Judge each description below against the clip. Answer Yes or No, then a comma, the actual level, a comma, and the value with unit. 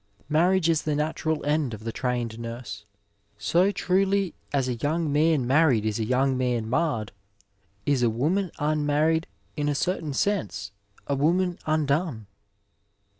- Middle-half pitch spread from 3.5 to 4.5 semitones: No, average, 4.9 semitones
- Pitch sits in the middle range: Yes, medium, 145 Hz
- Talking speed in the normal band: Yes, average, 145 wpm